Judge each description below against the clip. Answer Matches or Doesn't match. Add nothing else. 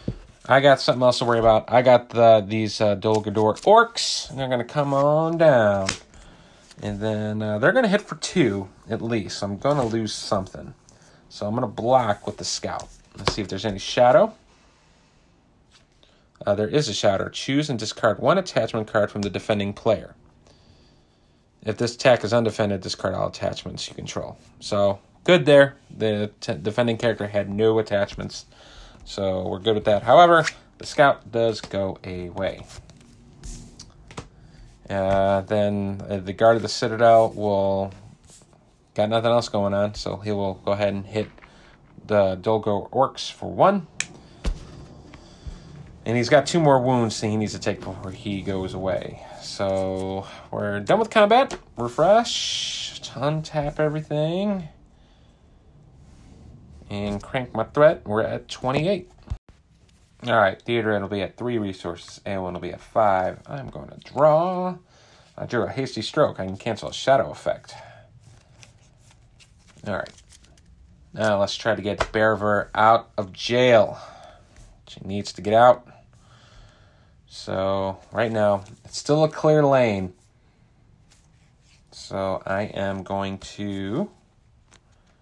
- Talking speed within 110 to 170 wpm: Matches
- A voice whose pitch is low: Matches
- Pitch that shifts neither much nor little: Matches